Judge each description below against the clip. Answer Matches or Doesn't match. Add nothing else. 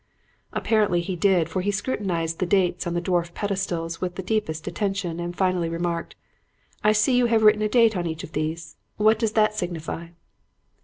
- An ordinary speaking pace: Matches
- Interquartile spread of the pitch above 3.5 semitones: Matches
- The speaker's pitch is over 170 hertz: Matches